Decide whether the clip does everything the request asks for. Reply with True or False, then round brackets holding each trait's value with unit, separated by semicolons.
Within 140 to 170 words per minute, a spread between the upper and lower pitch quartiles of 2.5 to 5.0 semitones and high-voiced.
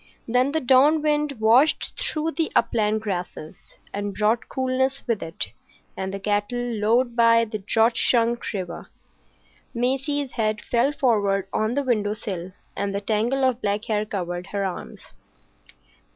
True (150 wpm; 3.9 semitones; 230 Hz)